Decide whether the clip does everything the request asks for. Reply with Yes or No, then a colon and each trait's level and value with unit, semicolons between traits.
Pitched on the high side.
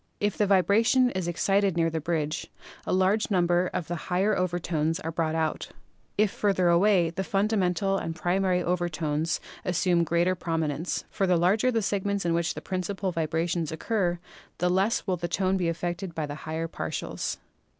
No: medium, 180 Hz